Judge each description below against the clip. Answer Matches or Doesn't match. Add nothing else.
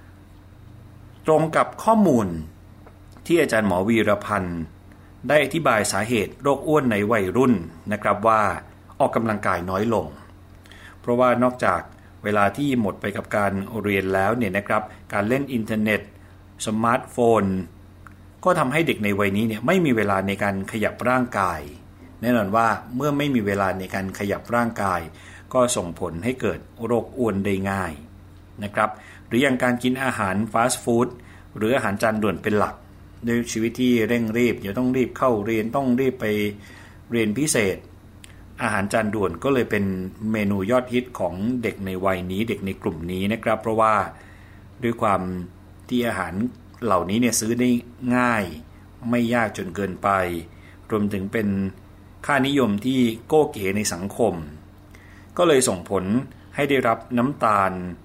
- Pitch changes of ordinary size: Matches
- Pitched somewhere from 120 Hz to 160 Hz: Doesn't match